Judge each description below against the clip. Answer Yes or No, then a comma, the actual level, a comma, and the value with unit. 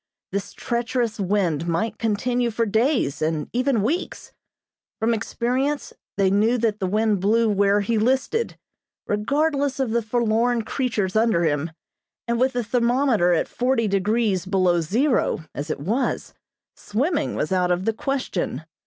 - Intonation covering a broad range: No, average, 4.0 semitones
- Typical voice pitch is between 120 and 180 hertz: No, high, 220 Hz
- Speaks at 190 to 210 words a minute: No, average, 145 wpm